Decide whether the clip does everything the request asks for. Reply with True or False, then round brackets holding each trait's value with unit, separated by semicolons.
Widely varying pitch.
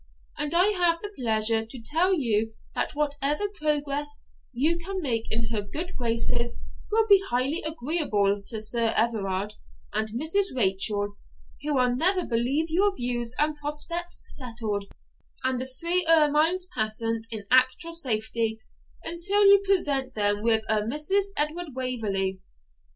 True (6.7 semitones)